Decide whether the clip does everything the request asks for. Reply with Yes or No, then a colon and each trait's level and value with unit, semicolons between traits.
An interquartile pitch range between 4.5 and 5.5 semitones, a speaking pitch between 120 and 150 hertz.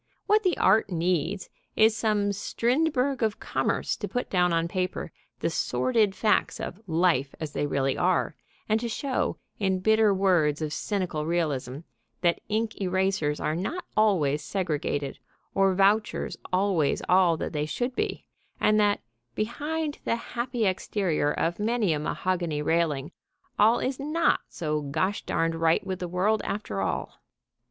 No: average, 5.0 semitones; high, 190 Hz